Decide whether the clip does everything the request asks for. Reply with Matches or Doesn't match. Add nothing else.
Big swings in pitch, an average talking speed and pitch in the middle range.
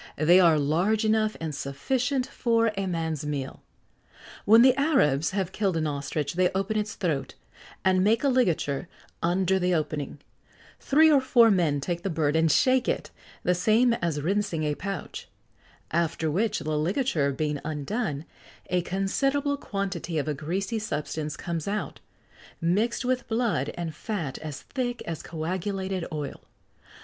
Matches